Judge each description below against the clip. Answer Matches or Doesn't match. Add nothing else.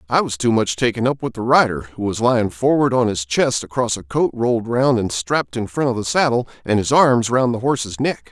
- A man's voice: Matches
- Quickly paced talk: Matches